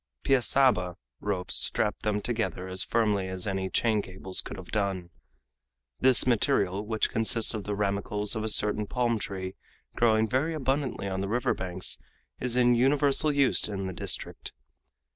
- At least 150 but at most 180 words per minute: Yes, average, 160 wpm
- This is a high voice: No, low, 105 Hz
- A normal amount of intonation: Yes, average, 4.2 semitones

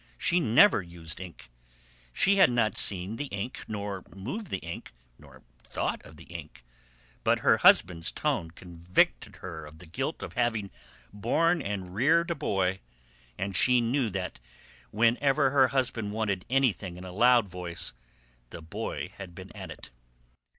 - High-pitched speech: No, low, 100 Hz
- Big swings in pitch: Yes, wide, 6.0 semitones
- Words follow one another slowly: No, average, 155 wpm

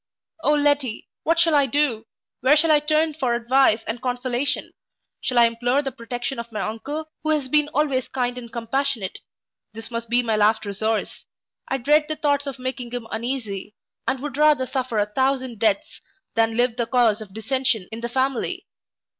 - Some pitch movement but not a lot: Yes, average, 3.7 semitones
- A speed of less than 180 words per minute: No, average, 185 wpm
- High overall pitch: Yes, very high, 250 Hz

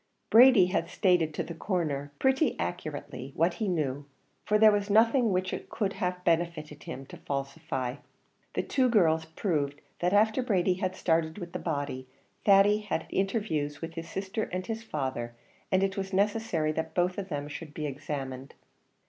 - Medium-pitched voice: Yes, medium, 175 Hz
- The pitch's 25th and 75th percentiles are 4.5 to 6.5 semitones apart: Yes, average, 5.2 semitones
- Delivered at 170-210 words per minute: Yes, average, 175 wpm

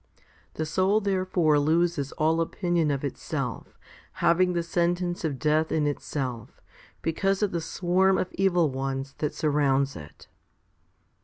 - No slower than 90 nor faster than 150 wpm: Yes, slow, 135 wpm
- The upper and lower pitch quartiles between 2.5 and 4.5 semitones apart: Yes, average, 3.6 semitones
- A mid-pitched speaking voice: Yes, medium, 165 Hz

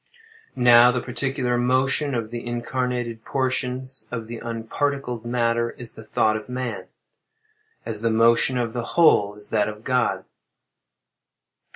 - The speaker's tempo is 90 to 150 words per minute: Yes, average, 140 wpm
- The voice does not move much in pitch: Yes, narrow, 1.8 semitones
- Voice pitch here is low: Yes, low, 120 Hz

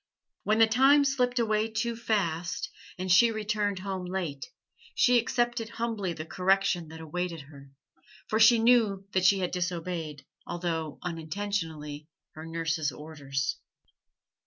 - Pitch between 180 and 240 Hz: Yes, medium, 185 Hz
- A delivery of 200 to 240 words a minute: No, slow, 135 wpm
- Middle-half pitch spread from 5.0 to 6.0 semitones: Yes, wide, 5.4 semitones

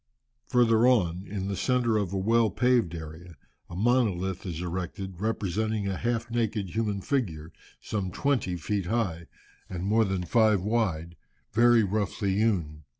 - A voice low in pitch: Yes, low, 100 Hz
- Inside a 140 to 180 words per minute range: Yes, average, 150 wpm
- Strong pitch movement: No, average, 4.3 semitones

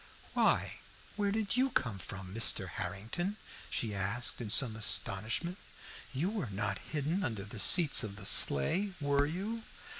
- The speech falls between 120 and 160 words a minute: Yes, average, 150 wpm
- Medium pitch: No, low, 125 Hz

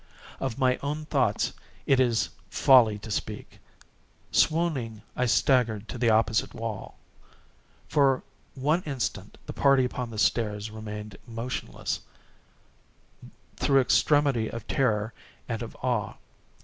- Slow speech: Yes, slow, 120 wpm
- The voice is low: Yes, low, 120 Hz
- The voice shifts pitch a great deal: No, average, 3.6 semitones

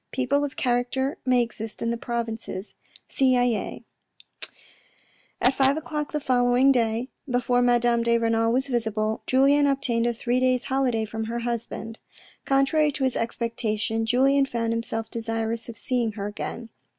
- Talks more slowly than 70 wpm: No, average, 150 wpm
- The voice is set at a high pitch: Yes, high, 240 Hz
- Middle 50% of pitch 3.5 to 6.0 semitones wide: No, narrow, 2.6 semitones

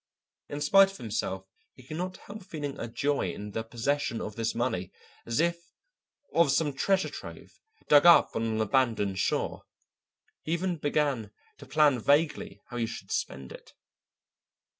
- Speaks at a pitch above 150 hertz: No, medium, 140 Hz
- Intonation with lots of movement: Yes, wide, 5.9 semitones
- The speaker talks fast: No, average, 160 wpm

